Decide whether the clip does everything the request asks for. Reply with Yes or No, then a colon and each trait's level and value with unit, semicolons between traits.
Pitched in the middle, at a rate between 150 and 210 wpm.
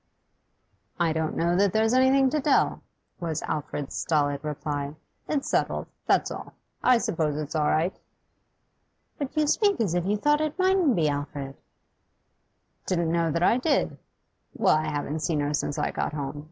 Yes: medium, 165 Hz; average, 165 wpm